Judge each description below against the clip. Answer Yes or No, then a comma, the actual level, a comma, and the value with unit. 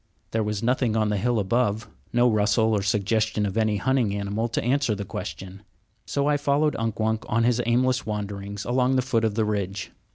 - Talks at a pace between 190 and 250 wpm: Yes, average, 200 wpm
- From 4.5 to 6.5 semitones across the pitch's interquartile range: No, average, 3.1 semitones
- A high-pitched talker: No, low, 110 Hz